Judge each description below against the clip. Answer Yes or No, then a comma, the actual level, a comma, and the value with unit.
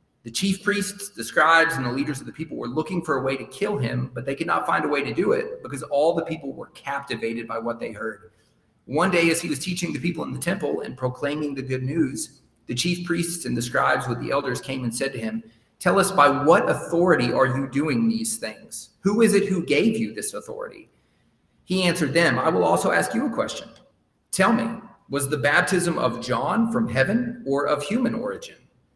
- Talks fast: Yes, fast, 230 wpm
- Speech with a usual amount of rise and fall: No, wide, 6.7 semitones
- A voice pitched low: No, medium, 165 Hz